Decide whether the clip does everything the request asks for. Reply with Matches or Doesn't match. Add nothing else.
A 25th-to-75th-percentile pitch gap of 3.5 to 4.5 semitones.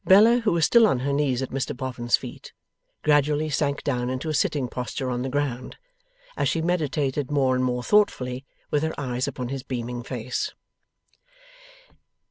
Doesn't match